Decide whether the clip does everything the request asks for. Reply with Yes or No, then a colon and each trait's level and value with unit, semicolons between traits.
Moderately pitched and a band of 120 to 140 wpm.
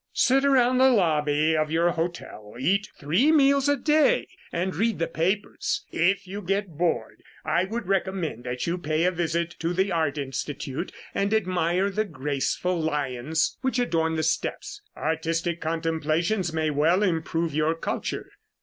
No: medium, 170 Hz; average, 155 wpm